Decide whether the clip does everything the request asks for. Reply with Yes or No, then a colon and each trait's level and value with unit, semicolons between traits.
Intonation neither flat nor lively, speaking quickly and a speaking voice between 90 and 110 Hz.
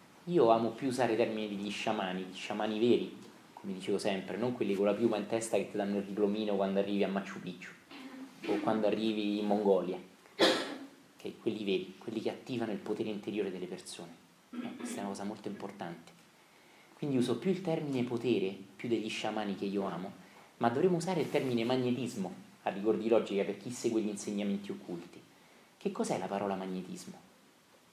Yes: average, 3.5 semitones; fast, 185 wpm; low, 105 Hz